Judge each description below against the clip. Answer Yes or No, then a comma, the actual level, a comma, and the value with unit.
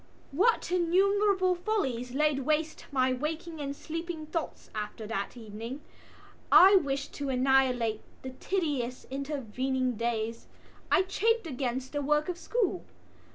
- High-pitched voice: Yes, very high, 280 Hz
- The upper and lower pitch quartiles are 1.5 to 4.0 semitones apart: No, wide, 5.5 semitones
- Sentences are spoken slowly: Yes, slow, 125 wpm